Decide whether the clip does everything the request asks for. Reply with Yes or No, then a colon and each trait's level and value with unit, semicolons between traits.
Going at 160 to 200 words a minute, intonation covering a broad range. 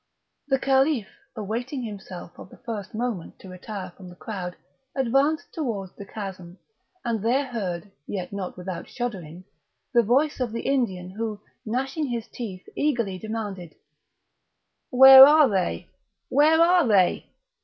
No: average, 140 wpm; wide, 5.8 semitones